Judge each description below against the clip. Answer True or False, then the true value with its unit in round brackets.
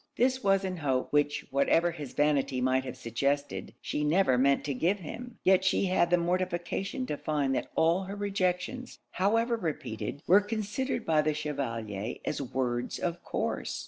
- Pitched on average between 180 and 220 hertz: False (160 Hz)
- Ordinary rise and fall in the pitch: False (5.9 semitones)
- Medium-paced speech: True (170 wpm)